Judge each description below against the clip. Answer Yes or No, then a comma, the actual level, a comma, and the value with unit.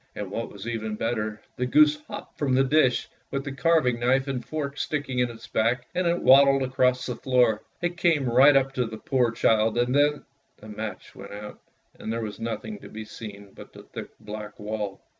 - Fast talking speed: Yes, fast, 215 wpm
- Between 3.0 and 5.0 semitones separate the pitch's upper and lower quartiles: Yes, average, 4.0 semitones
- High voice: No, low, 125 Hz